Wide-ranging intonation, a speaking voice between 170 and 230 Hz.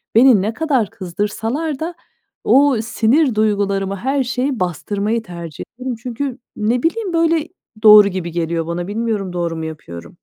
Yes: wide, 6.1 semitones; high, 220 Hz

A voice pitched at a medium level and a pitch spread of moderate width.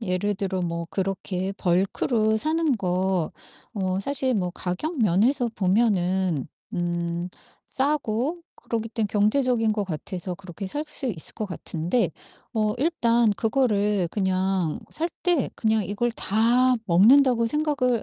No: high, 210 Hz; average, 4.8 semitones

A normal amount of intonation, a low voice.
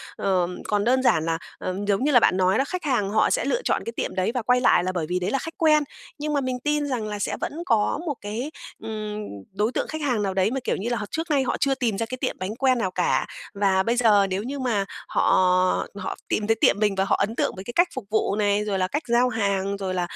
No: average, 4.8 semitones; high, 220 Hz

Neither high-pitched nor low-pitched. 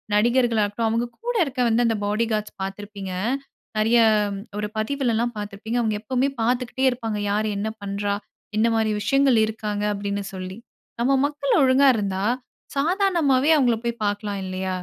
No: high, 225 Hz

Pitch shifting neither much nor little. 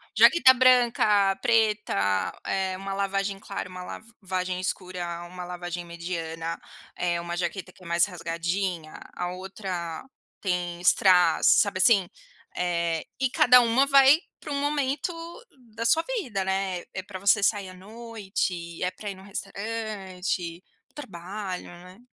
Yes: average, 3.4 semitones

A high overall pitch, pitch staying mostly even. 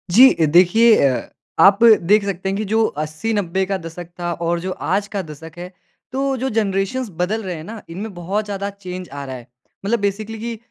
No: high, 195 Hz; average, 3.8 semitones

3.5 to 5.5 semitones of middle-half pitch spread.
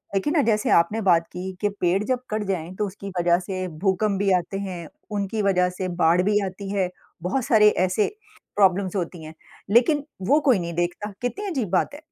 No: average, 2.8 semitones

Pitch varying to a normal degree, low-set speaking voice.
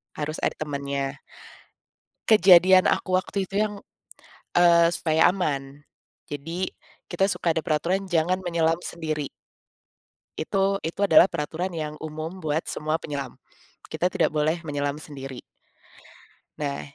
No: average, 3.5 semitones; medium, 160 Hz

